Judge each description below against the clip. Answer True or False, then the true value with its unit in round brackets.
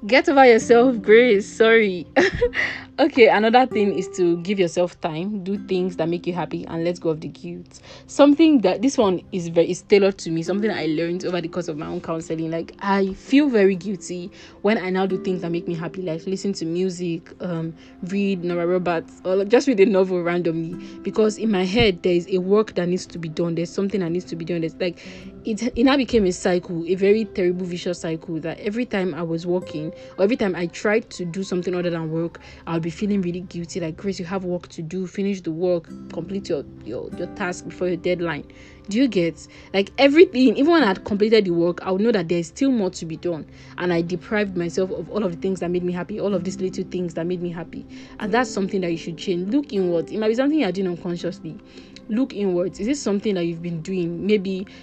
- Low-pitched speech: False (185 Hz)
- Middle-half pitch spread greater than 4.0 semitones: False (3.1 semitones)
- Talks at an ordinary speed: False (240 wpm)